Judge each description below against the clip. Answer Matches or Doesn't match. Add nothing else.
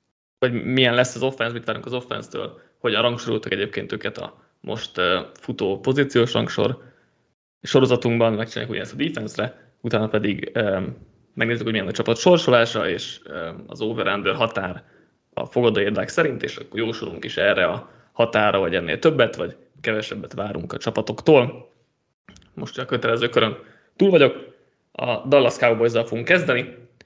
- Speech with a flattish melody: Matches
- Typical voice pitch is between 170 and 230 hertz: Doesn't match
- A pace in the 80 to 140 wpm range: Doesn't match